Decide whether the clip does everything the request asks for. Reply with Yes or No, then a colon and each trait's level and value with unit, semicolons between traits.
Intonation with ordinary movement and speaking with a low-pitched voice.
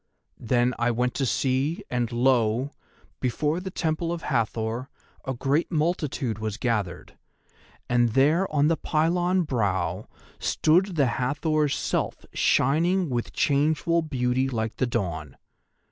Yes: average, 4.9 semitones; low, 130 Hz